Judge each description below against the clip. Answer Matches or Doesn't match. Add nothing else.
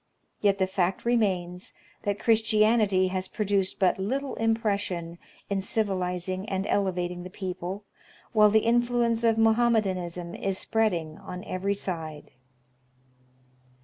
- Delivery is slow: Matches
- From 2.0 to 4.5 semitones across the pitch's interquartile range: Matches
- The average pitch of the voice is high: Matches